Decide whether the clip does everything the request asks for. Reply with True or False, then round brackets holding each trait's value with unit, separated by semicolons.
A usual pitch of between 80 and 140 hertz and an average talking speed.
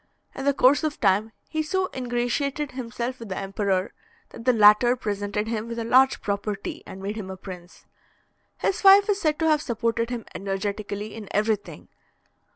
False (230 Hz; 175 wpm)